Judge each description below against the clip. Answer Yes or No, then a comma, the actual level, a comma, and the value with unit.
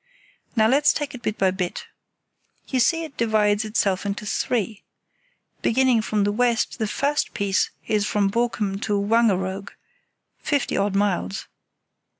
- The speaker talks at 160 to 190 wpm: No, average, 140 wpm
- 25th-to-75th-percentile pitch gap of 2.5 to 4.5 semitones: Yes, average, 3.0 semitones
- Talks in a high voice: Yes, high, 215 Hz